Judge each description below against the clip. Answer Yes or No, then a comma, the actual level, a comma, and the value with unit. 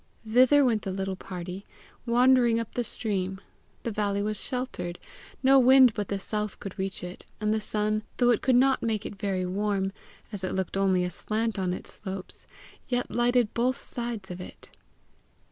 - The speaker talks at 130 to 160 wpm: No, average, 180 wpm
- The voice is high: Yes, high, 210 Hz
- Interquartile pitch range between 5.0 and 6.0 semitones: No, average, 3.9 semitones